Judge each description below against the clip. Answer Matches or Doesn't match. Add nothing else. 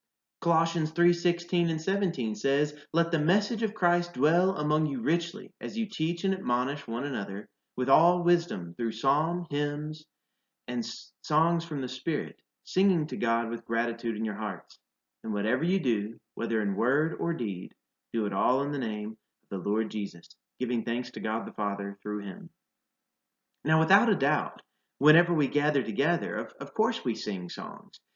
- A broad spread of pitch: Matches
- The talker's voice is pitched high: Doesn't match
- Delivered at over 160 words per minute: Matches